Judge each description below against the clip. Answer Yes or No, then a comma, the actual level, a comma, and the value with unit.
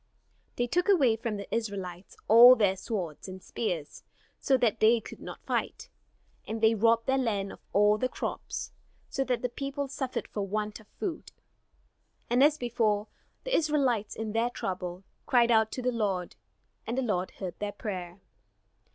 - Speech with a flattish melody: No, average, 3.7 semitones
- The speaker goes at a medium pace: Yes, average, 170 wpm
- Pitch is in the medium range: No, high, 225 Hz